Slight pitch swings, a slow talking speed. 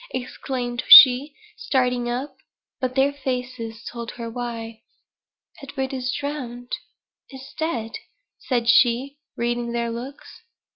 Yes: narrow, 2.1 semitones; slow, 110 wpm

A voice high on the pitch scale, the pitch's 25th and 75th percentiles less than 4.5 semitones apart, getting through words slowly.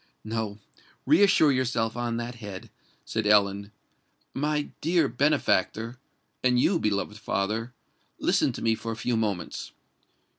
No: low, 115 Hz; average, 3.5 semitones; slow, 110 wpm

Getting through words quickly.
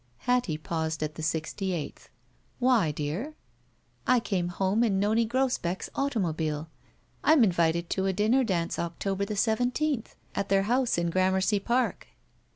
No: average, 150 wpm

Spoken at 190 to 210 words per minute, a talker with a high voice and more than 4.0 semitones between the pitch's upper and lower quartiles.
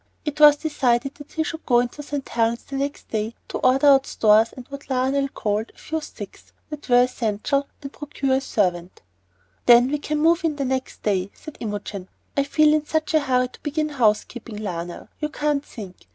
Yes: average, 200 wpm; very high, 270 Hz; average, 4.7 semitones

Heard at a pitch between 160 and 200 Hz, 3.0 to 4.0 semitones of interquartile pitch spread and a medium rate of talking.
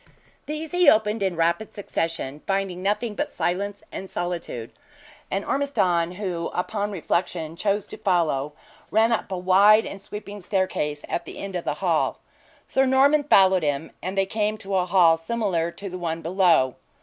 Yes: high, 190 Hz; average, 3.5 semitones; average, 170 wpm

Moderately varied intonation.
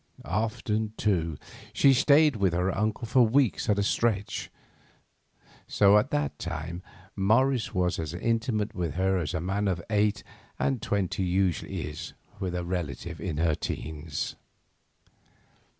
Yes: average, 4.1 semitones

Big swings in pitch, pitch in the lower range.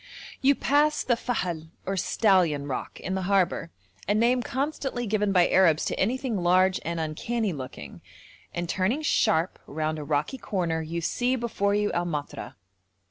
No: wide, 6.4 semitones; high, 190 Hz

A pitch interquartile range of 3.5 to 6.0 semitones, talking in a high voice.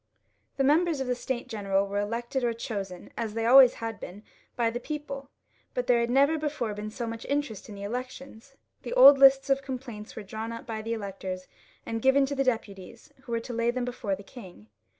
Yes: average, 4.1 semitones; high, 235 Hz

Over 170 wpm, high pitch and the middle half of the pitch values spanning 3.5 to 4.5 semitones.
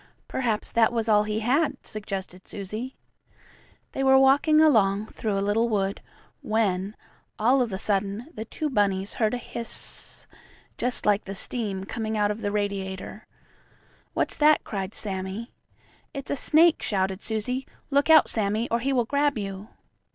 No: average, 160 wpm; high, 215 Hz; average, 3.9 semitones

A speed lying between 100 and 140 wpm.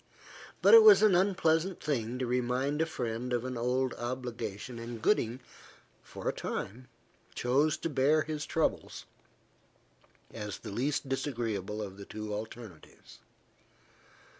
Yes: slow, 135 wpm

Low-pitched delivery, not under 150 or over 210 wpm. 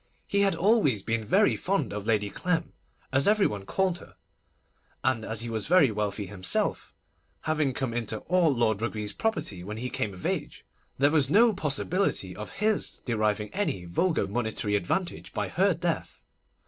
Yes: low, 125 Hz; average, 170 wpm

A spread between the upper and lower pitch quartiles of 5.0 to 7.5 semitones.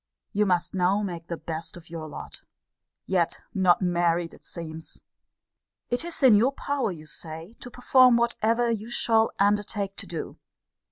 Yes: average, 5.3 semitones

